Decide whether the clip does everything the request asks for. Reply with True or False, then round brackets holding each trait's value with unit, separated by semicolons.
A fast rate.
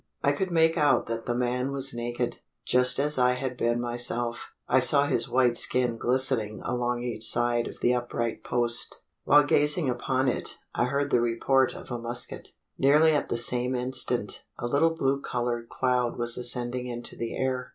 False (185 wpm)